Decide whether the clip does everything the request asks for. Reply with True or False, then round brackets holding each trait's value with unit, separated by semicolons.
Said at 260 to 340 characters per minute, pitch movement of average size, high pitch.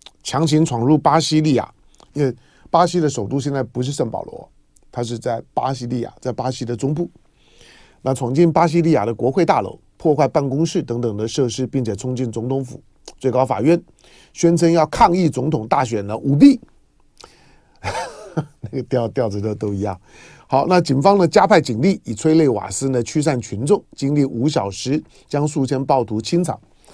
False (265 characters per minute; 4.8 semitones; 135 Hz)